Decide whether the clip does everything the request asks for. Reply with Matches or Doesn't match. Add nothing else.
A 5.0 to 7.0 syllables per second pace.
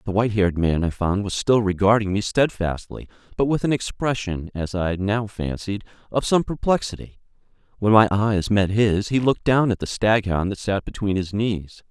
Matches